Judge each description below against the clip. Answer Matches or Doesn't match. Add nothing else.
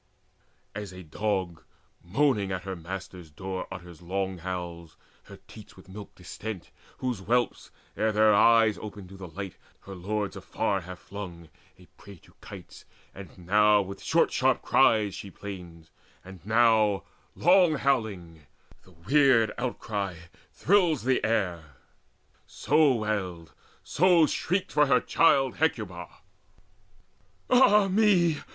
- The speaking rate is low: Matches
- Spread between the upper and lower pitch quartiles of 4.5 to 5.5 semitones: Matches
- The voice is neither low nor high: Doesn't match